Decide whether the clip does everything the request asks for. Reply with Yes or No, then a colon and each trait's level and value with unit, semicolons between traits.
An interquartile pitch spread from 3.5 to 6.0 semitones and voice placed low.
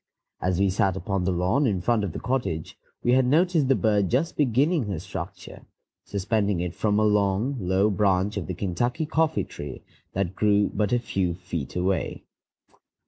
Yes: average, 4.8 semitones; low, 100 Hz